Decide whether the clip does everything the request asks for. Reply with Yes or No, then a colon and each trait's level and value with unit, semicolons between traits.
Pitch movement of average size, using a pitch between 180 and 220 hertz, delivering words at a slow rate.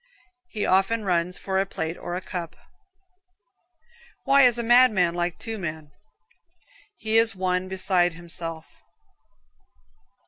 Yes: average, 4.0 semitones; medium, 185 Hz; slow, 125 wpm